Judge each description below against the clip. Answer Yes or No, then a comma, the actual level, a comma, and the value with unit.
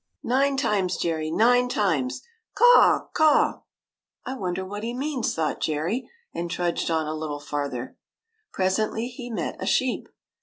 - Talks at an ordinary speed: Yes, average, 160 wpm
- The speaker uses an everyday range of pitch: No, wide, 7.6 semitones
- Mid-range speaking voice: No, high, 195 Hz